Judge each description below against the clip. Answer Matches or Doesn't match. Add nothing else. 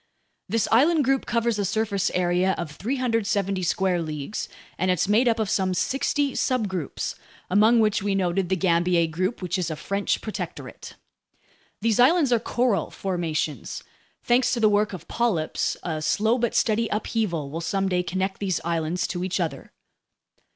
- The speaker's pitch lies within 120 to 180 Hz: Doesn't match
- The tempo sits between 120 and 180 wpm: Matches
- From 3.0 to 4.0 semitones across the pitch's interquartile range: Doesn't match